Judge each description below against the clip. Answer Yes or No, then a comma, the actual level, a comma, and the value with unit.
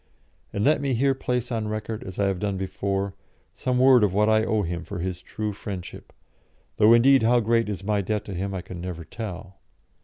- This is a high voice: No, low, 105 Hz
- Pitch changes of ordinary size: Yes, average, 3.2 semitones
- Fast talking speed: Yes, fast, 215 wpm